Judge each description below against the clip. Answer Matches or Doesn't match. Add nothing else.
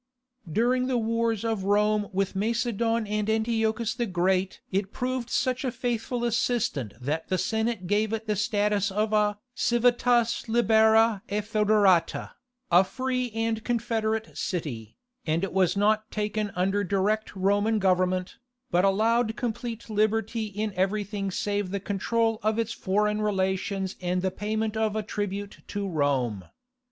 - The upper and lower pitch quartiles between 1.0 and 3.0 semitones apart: Matches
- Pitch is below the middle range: Doesn't match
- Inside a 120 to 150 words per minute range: Matches